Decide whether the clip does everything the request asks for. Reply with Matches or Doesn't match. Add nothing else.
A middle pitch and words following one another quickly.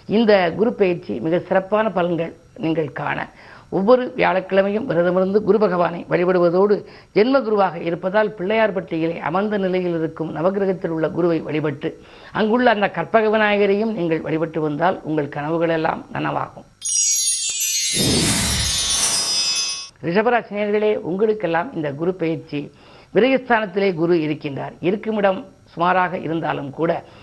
Doesn't match